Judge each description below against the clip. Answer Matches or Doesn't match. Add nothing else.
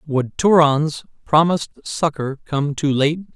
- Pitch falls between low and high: Matches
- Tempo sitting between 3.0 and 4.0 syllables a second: Matches